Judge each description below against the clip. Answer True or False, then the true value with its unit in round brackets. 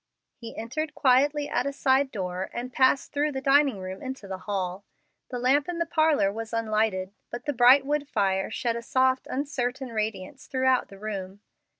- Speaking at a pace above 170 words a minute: True (185 wpm)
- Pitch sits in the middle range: False (250 Hz)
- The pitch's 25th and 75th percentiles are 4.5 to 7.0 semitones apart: True (5.2 semitones)